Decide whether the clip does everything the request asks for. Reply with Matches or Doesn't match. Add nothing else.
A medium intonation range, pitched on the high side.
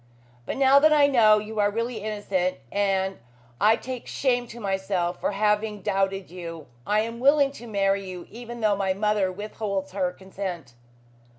Matches